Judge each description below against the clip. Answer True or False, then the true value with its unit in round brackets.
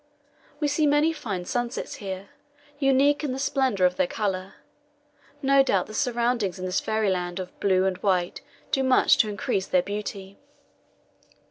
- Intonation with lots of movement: True (6.0 semitones)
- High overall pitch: True (210 Hz)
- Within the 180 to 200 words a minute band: False (155 wpm)